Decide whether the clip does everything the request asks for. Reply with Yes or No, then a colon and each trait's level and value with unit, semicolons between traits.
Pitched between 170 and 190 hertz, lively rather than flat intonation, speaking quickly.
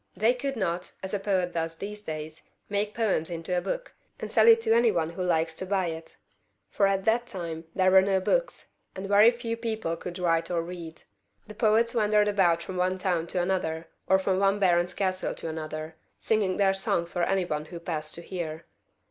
No: medium, 185 Hz; average, 3.6 semitones; fast, 215 wpm